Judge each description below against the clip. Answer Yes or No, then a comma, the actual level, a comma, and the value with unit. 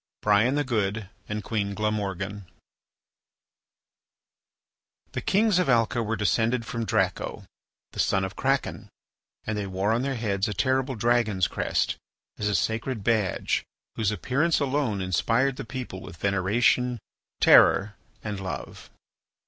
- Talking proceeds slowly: Yes, slow, 130 wpm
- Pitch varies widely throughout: No, average, 3.8 semitones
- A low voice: Yes, low, 110 Hz